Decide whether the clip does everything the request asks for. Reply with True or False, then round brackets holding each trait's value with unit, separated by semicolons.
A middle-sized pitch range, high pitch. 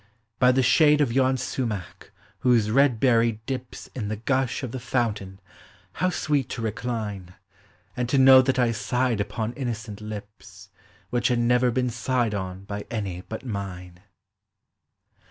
False (3.8 semitones; 115 Hz)